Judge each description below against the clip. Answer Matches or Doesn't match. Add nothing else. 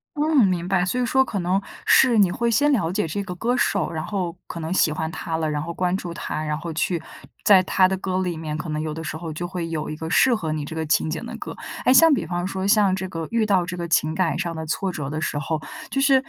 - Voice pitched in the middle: Matches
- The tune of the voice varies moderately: Matches